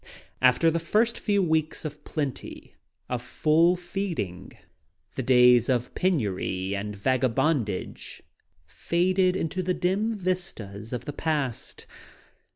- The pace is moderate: No, slow, 115 wpm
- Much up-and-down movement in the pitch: Yes, wide, 7.1 semitones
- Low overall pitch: No, medium, 150 Hz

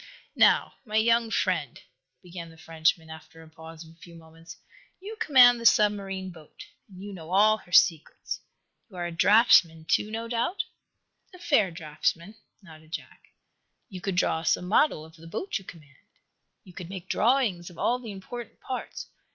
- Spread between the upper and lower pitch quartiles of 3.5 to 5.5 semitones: Yes, average, 5.0 semitones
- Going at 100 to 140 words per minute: No, average, 175 wpm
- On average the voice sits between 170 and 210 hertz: Yes, medium, 185 Hz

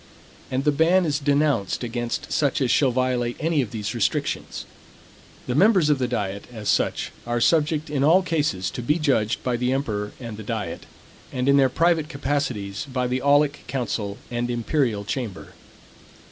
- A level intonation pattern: No, average, 3.8 semitones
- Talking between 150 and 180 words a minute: Yes, average, 170 wpm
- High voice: No, low, 130 Hz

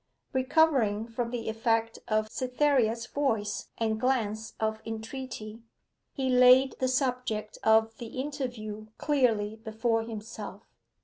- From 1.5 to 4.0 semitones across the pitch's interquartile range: Yes, average, 2.9 semitones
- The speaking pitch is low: No, high, 225 Hz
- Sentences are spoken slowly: Yes, slow, 115 wpm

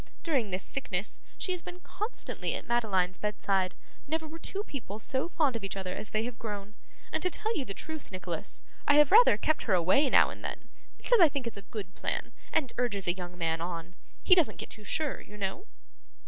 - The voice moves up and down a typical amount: No, wide, 8.6 semitones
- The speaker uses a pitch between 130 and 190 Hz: No, high, 230 Hz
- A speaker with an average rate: No, fast, 220 wpm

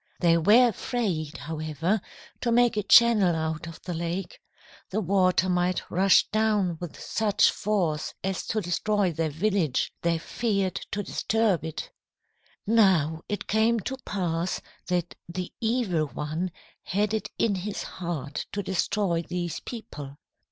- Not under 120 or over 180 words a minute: Yes, average, 140 wpm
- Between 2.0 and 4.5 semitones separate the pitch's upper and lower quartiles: Yes, average, 4.2 semitones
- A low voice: No, medium, 185 Hz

